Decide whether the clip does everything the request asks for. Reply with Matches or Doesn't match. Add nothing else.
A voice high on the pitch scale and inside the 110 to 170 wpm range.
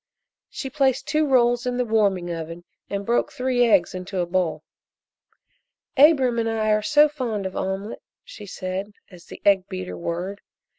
Matches